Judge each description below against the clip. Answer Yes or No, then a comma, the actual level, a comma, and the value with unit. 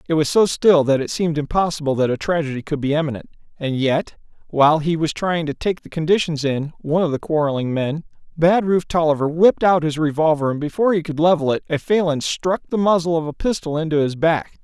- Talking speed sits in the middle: No, fast, 215 wpm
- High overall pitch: No, medium, 160 Hz